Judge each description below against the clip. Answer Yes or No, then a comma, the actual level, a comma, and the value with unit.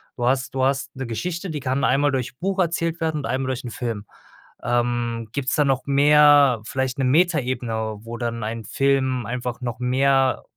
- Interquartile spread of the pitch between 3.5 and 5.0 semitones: No, average, 2.8 semitones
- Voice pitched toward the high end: No, low, 130 Hz